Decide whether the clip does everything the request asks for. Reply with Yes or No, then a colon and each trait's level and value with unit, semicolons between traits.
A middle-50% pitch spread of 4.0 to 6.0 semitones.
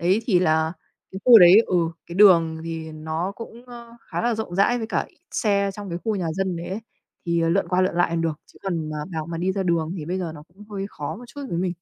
No: average, 3.4 semitones